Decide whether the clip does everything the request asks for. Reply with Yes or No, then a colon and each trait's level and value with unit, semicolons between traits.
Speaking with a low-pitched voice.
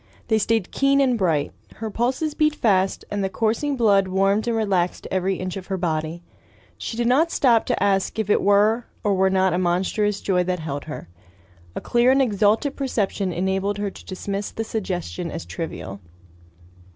No: high, 200 Hz